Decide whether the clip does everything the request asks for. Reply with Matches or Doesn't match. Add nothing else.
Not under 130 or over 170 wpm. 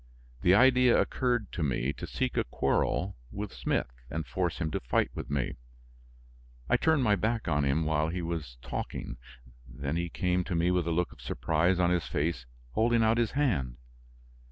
Doesn't match